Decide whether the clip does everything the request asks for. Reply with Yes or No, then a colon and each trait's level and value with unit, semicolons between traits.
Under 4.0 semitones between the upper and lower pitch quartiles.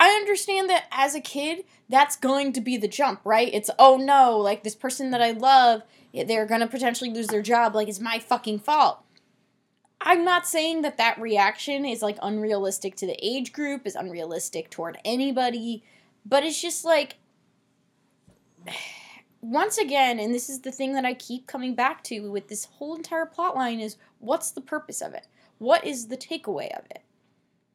No: average, 4.8 semitones